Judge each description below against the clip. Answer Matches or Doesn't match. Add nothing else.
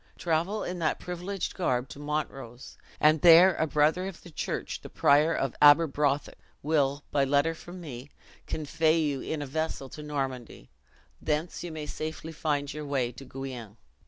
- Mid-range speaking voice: Matches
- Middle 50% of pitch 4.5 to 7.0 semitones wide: Doesn't match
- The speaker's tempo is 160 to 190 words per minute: Matches